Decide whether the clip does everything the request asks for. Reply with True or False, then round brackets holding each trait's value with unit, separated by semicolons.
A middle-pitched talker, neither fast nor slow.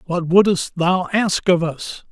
True (180 Hz; 170 wpm)